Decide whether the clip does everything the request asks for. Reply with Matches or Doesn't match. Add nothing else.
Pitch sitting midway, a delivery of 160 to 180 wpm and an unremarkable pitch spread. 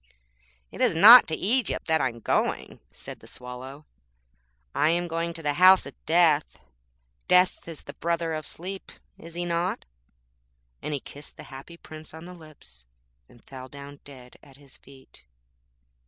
Matches